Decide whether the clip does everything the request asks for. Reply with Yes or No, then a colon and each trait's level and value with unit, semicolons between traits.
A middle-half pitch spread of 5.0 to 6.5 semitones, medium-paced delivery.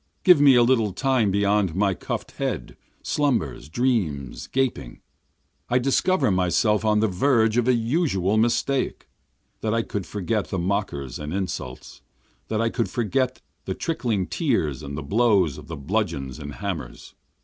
Yes: wide, 5.6 semitones; average, 155 wpm